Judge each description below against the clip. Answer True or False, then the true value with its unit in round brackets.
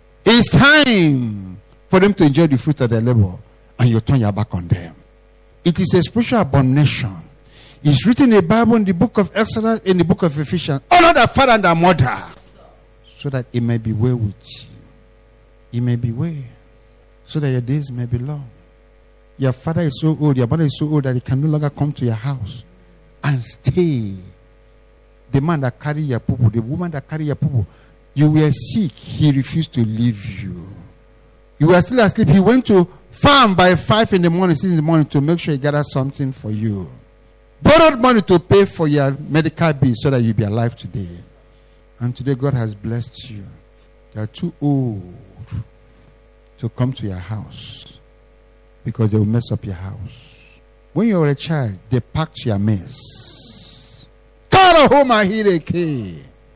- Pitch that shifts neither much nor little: False (5.9 semitones)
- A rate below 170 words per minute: False (190 wpm)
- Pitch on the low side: True (130 Hz)